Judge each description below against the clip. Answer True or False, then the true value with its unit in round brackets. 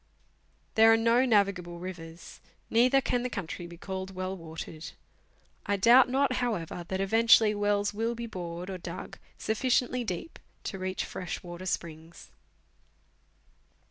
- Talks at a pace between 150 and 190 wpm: False (140 wpm)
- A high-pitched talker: True (195 Hz)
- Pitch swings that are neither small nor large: True (4.7 semitones)